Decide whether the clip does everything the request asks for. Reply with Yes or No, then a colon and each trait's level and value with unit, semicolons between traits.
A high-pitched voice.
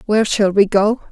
Yes: high, 205 Hz